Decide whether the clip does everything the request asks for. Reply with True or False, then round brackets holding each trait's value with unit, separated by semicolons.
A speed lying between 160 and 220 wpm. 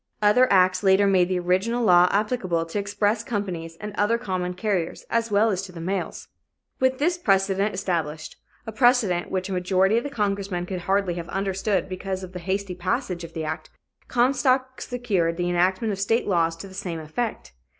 True (190 wpm)